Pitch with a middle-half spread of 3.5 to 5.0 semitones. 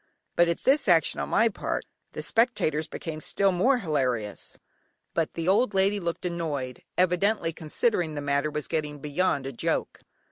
Yes: average, 4.4 semitones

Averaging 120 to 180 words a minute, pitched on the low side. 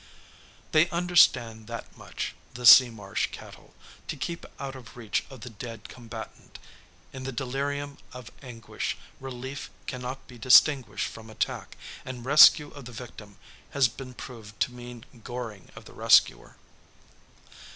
Yes: average, 140 wpm; low, 125 Hz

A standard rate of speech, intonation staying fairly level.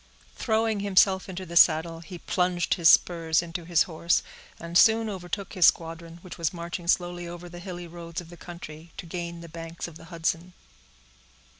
Yes: average, 180 wpm; narrow, 1.3 semitones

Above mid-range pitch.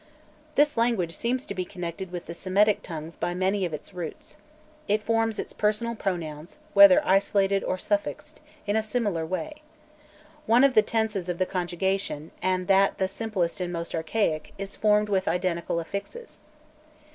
Yes: high, 195 Hz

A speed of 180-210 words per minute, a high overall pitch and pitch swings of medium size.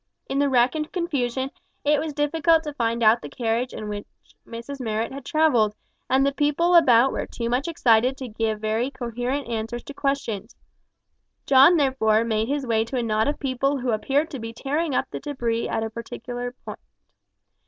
Yes: average, 190 wpm; very high, 255 Hz; average, 3.8 semitones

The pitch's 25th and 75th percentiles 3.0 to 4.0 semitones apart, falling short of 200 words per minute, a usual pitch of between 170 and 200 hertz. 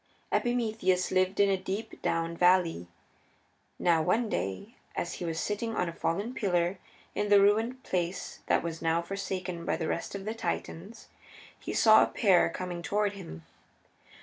Yes: average, 3.4 semitones; average, 165 wpm; medium, 185 Hz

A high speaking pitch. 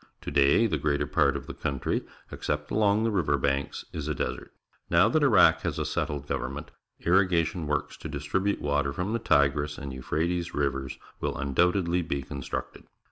No: very low, 75 Hz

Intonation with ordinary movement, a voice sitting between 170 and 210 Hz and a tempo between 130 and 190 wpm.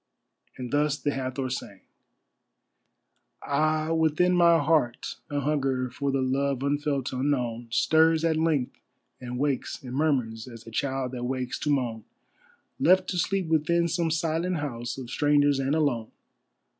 No: average, 3.7 semitones; medium, 140 Hz; average, 145 wpm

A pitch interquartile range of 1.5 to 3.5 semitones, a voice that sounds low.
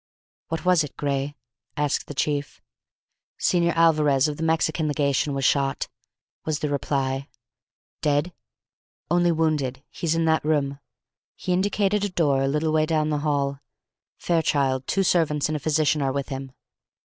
No: narrow, 2.6 semitones; medium, 150 Hz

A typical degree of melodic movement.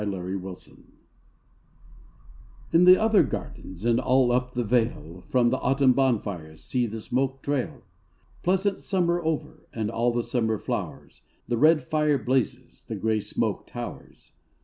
Yes: average, 4.6 semitones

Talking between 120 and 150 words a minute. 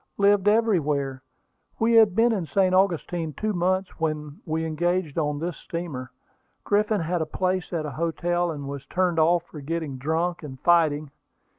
No: average, 165 wpm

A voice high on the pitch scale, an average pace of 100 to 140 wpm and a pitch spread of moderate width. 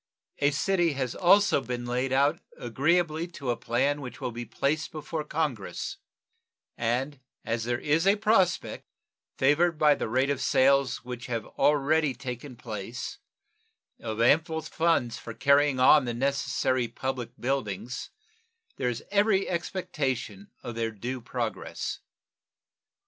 No: low, 135 Hz; slow, 135 wpm; average, 4.2 semitones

